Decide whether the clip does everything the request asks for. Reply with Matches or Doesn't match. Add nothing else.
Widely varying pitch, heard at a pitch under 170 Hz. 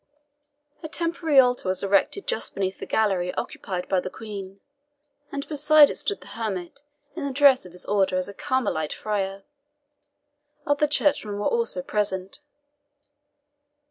Doesn't match